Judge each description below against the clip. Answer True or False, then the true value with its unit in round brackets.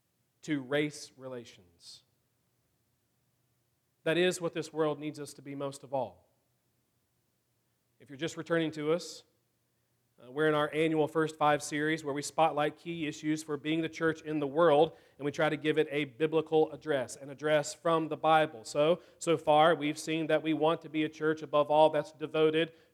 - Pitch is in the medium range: True (155 Hz)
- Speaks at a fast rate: False (185 wpm)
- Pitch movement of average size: False (1.5 semitones)